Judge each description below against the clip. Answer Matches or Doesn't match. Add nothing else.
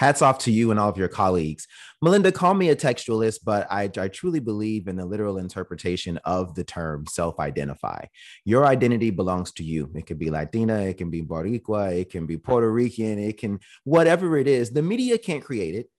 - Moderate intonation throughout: Doesn't match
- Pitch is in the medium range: Doesn't match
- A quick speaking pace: Matches